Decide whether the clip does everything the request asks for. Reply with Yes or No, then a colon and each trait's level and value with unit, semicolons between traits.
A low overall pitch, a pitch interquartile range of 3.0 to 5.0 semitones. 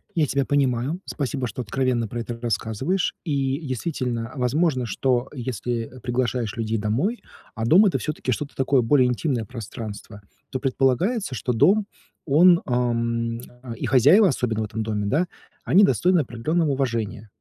Yes: low, 125 Hz; average, 3.9 semitones